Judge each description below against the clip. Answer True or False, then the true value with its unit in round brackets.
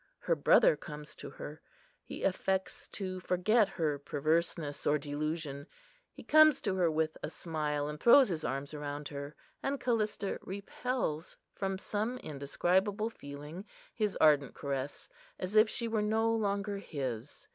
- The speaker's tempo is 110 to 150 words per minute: True (145 wpm)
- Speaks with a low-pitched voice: False (175 Hz)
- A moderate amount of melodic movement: False (6.1 semitones)